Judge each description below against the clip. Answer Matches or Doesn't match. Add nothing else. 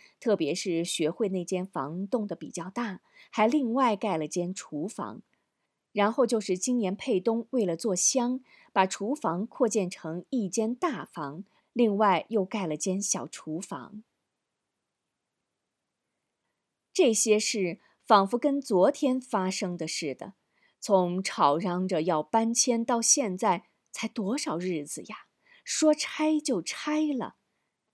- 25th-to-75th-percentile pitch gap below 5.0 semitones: Doesn't match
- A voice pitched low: Doesn't match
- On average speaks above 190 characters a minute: Doesn't match